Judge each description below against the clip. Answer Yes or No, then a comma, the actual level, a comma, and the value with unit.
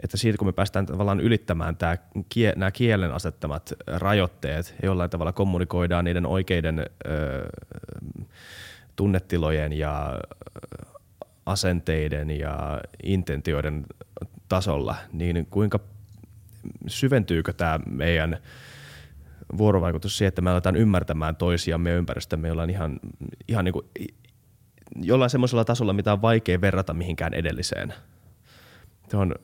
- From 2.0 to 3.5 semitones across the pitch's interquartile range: No, average, 4.2 semitones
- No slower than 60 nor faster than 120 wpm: Yes, average, 110 wpm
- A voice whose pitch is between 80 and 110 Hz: Yes, very low, 90 Hz